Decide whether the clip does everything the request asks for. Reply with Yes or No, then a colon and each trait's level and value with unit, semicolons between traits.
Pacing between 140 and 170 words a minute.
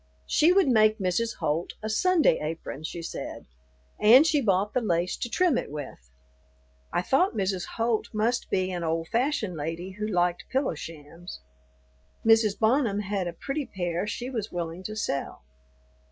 Yes: average, 165 wpm